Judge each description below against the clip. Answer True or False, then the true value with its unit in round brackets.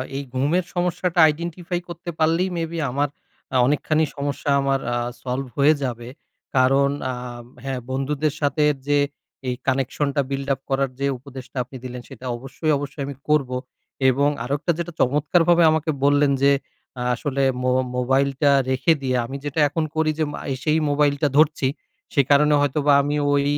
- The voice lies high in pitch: False (140 Hz)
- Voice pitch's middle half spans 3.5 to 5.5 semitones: False (2.4 semitones)